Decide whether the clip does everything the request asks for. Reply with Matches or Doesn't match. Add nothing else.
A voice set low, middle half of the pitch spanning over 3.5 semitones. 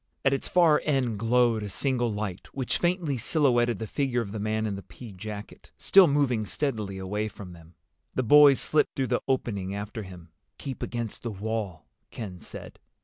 Matches